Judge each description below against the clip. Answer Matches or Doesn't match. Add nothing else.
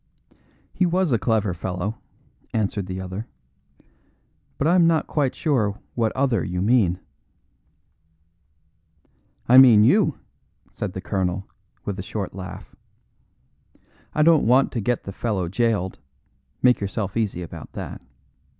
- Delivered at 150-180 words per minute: Doesn't match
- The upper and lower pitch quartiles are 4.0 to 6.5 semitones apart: Matches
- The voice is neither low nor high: Doesn't match